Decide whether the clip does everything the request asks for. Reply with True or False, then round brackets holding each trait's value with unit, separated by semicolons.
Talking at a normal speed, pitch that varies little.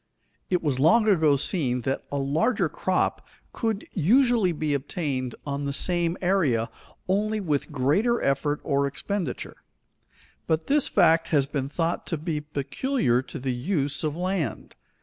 False (150 wpm; 5.1 semitones)